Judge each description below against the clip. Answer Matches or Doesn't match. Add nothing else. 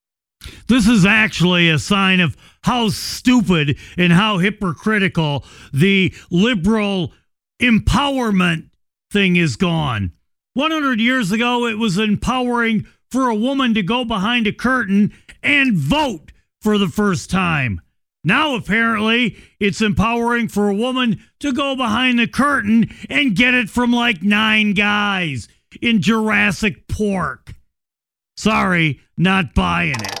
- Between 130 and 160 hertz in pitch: Doesn't match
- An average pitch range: Matches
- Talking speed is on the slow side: Matches